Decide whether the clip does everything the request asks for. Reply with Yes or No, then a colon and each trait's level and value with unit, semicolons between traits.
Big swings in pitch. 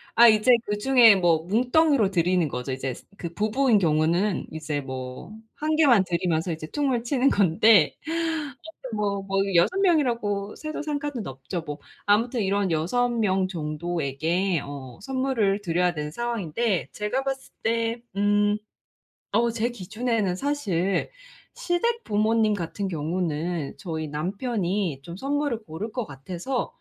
Yes: wide, 6.2 semitones